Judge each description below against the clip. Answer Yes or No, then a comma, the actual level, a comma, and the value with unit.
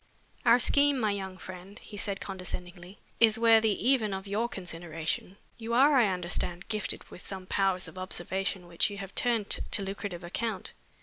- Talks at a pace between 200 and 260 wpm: No, average, 170 wpm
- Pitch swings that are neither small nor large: Yes, average, 3.5 semitones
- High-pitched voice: Yes, high, 195 Hz